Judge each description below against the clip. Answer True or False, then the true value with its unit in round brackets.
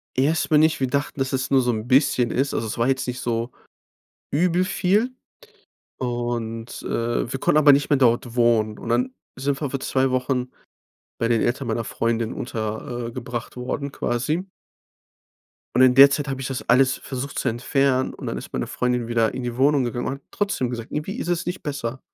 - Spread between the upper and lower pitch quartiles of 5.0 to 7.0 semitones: False (2.8 semitones)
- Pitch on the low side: True (130 Hz)